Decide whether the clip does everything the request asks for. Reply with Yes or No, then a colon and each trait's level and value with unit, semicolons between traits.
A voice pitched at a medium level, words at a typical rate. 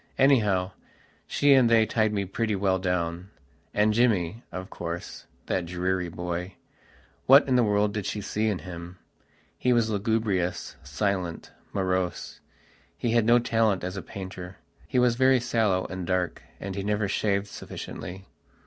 No: low, 100 Hz; average, 150 wpm